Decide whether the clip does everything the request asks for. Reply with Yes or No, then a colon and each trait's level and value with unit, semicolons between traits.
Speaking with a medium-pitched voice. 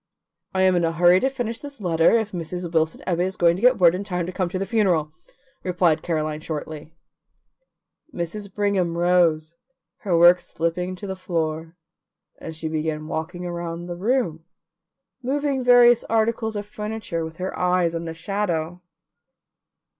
Yes: medium, 180 Hz